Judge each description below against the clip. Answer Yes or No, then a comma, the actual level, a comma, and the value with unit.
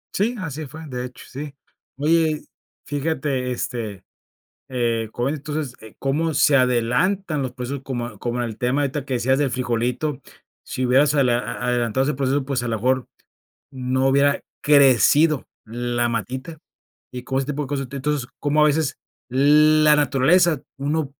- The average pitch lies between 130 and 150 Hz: Yes, low, 135 Hz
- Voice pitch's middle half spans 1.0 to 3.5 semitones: Yes, average, 3.2 semitones